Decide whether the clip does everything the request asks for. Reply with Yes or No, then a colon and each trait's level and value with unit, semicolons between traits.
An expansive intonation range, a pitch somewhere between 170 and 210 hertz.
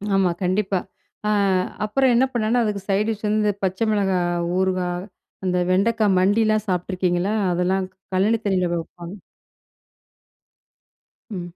No: average, 2.8 semitones; high, 190 Hz